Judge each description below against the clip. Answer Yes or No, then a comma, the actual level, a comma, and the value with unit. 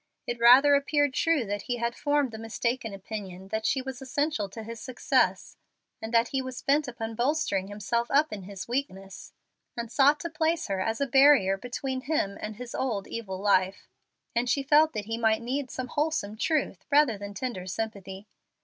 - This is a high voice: Yes, high, 235 Hz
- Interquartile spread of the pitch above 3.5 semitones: Yes, average, 5.0 semitones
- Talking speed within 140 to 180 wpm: No, average, 190 wpm